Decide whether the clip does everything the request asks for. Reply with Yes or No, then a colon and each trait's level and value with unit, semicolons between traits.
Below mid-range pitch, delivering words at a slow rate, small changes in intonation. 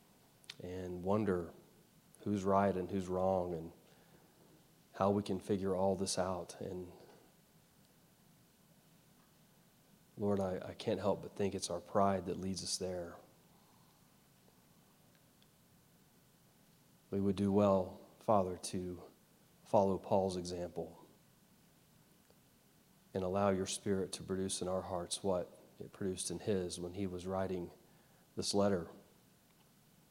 Yes: very low, 95 Hz; slow, 120 wpm; narrow, 1.6 semitones